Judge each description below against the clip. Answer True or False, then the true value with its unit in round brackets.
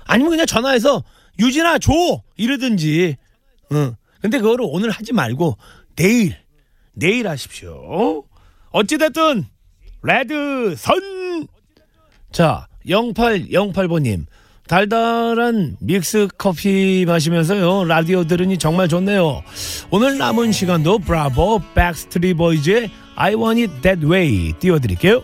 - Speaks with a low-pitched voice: False (185 Hz)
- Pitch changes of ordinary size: False (6.7 semitones)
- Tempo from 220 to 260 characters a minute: True (255 characters per minute)